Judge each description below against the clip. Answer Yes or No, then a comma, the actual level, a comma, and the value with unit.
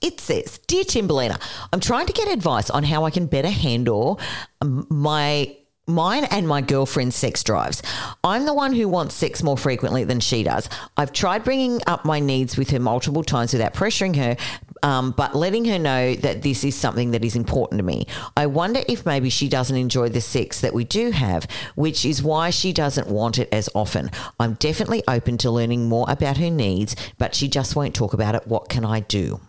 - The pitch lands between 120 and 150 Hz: Yes, medium, 140 Hz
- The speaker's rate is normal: No, fast, 210 wpm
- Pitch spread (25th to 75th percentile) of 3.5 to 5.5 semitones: Yes, average, 5.2 semitones